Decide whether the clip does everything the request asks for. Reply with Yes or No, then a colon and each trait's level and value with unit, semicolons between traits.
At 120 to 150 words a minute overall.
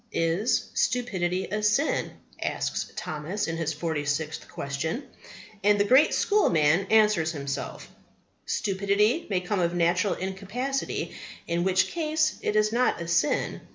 Yes: slow, 135 wpm